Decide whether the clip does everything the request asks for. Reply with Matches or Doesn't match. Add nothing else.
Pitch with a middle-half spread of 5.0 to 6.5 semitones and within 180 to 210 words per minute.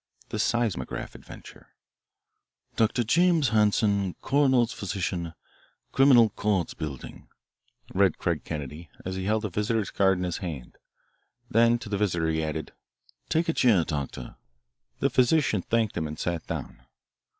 Doesn't match